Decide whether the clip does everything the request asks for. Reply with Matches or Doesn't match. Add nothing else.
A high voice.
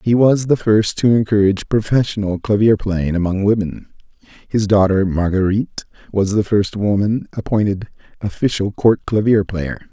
Doesn't match